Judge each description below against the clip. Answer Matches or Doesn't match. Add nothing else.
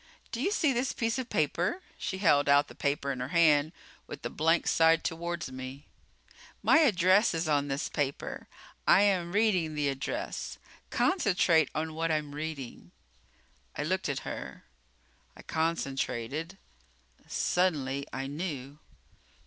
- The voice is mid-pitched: Matches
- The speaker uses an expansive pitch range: Doesn't match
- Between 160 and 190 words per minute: Doesn't match